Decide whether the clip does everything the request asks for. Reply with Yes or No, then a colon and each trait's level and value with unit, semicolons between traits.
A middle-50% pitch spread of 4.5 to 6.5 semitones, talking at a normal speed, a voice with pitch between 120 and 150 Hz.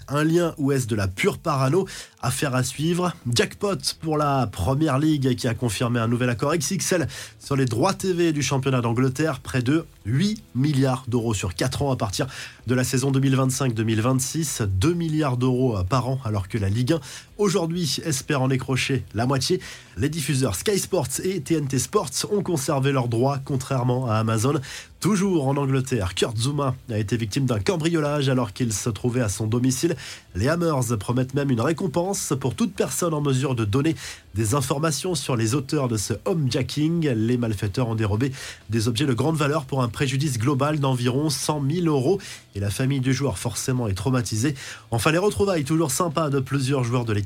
No: average, 4.1 semitones; average, 185 wpm; low, 135 Hz